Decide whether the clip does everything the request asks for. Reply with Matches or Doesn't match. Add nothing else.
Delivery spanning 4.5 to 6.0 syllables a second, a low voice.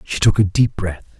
Matches